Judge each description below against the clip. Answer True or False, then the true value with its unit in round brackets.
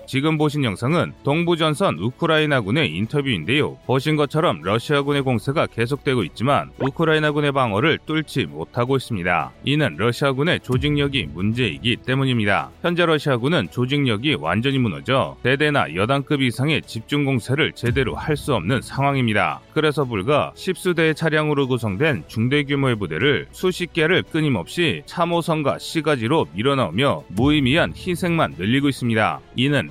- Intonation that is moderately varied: True (4.0 semitones)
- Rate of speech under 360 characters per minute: False (375 characters per minute)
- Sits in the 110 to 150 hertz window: True (140 Hz)